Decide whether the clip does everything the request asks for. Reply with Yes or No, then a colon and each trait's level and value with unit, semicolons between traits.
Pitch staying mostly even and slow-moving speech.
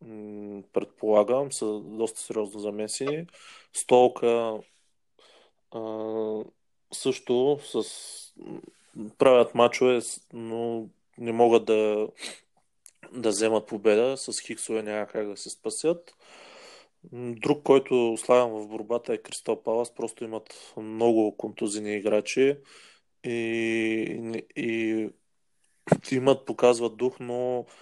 Yes: narrow, 2.1 semitones; slow, 95 wpm